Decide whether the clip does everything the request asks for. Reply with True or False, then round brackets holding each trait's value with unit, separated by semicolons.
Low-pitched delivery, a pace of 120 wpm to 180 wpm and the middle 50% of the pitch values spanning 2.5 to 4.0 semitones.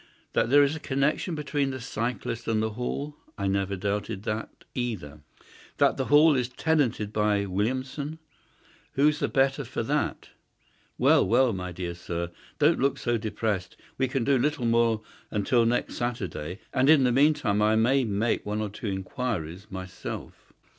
False (115 Hz; 165 wpm; 4.9 semitones)